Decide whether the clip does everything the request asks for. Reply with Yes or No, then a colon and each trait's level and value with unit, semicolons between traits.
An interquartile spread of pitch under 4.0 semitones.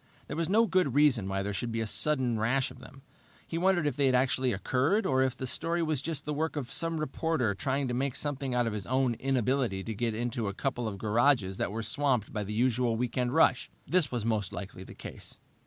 No: average, 4.3 semitones